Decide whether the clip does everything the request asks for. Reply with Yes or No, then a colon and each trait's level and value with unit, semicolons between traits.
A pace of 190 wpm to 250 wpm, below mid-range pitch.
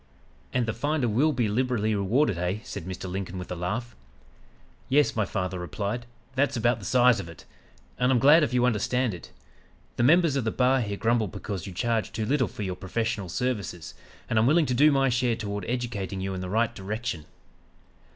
Yes: average, 200 wpm; low, 115 Hz